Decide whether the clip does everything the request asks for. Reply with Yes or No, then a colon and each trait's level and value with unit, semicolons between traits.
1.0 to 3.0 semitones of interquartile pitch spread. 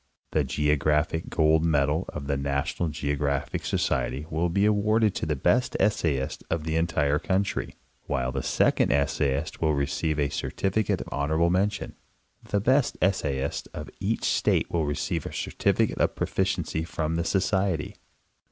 No: average, 4.6 semitones